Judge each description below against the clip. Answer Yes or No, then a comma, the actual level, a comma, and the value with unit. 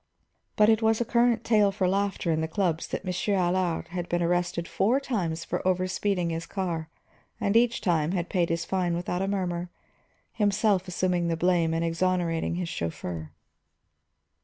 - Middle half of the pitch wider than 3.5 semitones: No, average, 3.0 semitones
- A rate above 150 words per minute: Yes, average, 175 wpm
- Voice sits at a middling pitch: Yes, medium, 180 Hz